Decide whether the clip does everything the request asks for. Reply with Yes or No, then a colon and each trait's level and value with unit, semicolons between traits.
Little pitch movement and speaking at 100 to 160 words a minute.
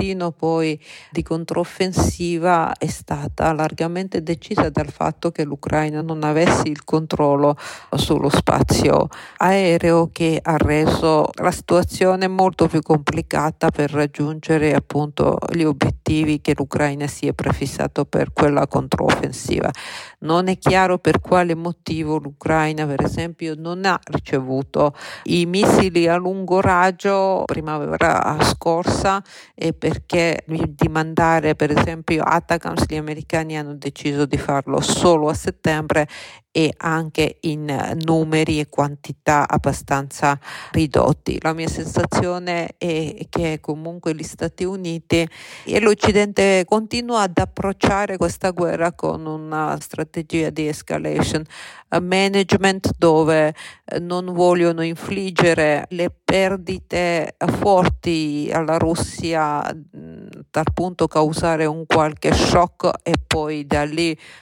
Yes: narrow, 2.3 semitones; slow, 115 wpm